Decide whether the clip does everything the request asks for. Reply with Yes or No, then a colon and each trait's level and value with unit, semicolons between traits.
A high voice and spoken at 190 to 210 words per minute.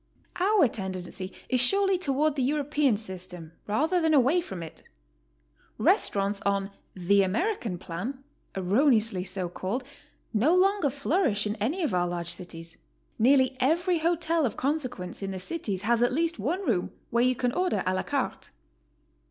No: high, 245 Hz; average, 155 wpm